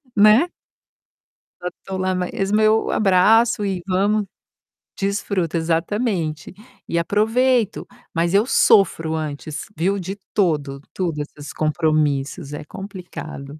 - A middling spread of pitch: Yes, average, 4.5 semitones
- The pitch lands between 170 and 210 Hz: Yes, medium, 185 Hz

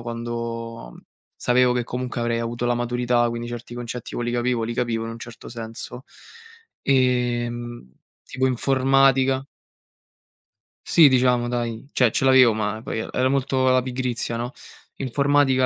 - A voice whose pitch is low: Yes, low, 120 Hz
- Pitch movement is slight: Yes, narrow, 1.6 semitones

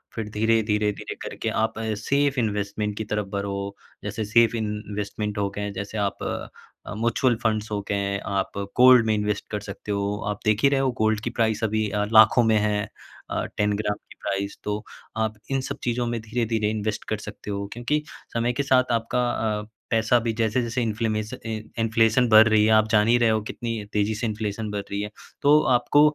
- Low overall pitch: Yes, low, 110 Hz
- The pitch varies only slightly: Yes, narrow, 1.9 semitones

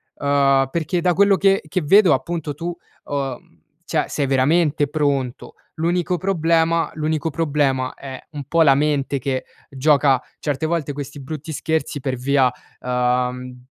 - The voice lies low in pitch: No, medium, 145 Hz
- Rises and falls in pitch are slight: No, average, 3.5 semitones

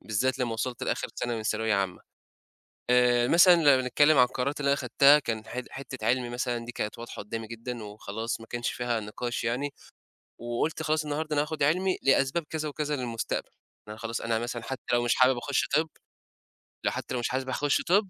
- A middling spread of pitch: Yes, average, 3.8 semitones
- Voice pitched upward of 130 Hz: No, low, 125 Hz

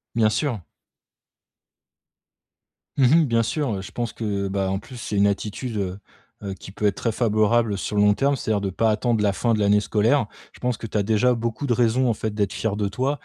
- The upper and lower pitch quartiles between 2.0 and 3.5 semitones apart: Yes, average, 2.8 semitones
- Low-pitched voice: Yes, low, 110 Hz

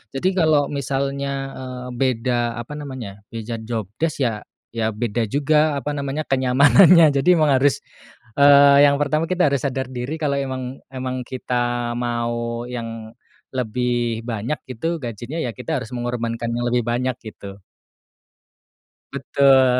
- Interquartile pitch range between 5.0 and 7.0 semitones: No, average, 2.8 semitones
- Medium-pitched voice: No, low, 130 Hz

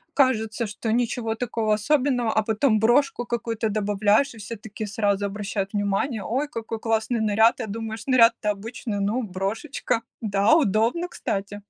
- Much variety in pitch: No, narrow, 2.5 semitones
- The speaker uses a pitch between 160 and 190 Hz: No, high, 220 Hz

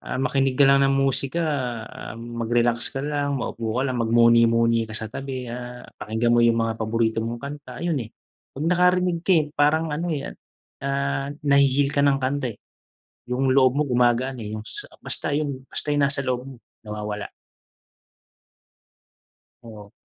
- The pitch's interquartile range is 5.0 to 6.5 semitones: No, average, 3.3 semitones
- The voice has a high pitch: No, low, 130 Hz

